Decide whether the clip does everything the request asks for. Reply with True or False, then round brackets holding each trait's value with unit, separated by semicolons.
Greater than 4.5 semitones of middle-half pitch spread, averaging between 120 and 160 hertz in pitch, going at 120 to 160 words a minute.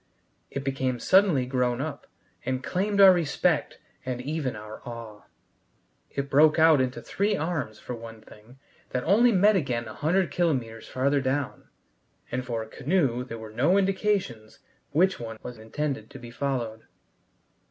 True (5.6 semitones; 135 Hz; 155 wpm)